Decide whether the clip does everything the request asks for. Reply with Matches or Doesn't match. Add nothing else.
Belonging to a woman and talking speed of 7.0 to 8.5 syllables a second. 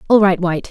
Matches